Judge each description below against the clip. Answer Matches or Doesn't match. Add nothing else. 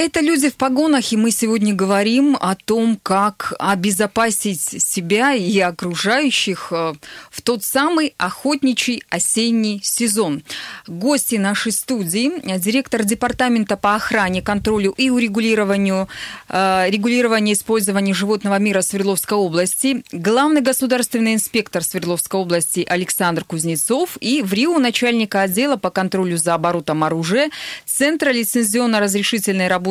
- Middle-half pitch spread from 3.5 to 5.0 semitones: Matches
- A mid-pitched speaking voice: Doesn't match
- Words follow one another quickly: Doesn't match